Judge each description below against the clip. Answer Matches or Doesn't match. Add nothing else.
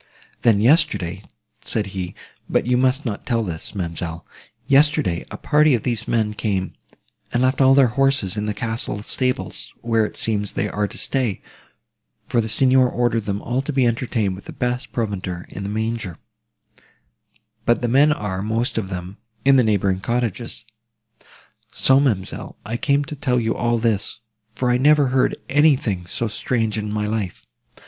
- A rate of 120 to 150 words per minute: Doesn't match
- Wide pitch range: Doesn't match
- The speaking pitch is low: Matches